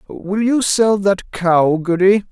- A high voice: Yes, high, 195 Hz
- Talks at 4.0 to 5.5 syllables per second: No, 3.4 syllables/s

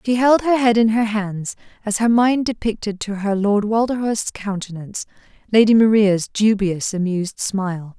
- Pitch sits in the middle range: No, high, 210 Hz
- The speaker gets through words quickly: No, average, 160 wpm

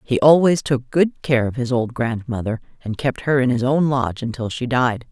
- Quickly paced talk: Yes, fast, 225 wpm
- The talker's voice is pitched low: Yes, low, 125 Hz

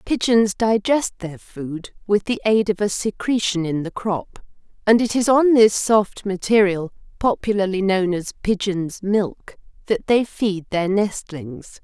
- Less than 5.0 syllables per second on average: Yes, 4.0 syllables/s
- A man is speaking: No, female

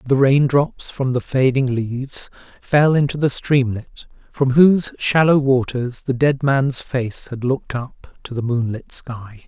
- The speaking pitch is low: Yes, low, 130 Hz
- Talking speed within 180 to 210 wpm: No, average, 165 wpm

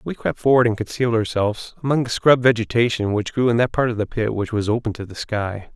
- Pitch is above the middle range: No, low, 115 Hz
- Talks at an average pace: No, fast, 250 wpm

